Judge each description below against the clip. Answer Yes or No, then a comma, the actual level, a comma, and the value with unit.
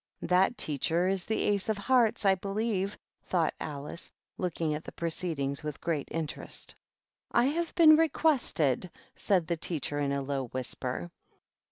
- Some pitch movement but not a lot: No, wide, 5.9 semitones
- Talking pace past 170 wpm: No, average, 165 wpm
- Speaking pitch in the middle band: Yes, medium, 175 Hz